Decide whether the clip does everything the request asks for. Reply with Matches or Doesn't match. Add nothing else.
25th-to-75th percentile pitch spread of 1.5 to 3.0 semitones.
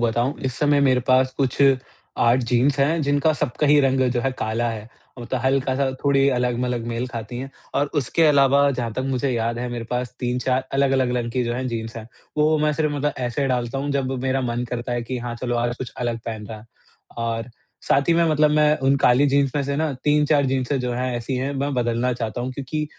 Matches